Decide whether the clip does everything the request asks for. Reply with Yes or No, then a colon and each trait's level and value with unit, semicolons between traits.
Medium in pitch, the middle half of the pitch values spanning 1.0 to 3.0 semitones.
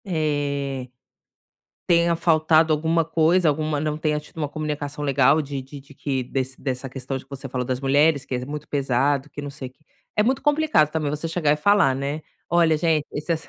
Yes: medium, 150 Hz; narrow, 2.6 semitones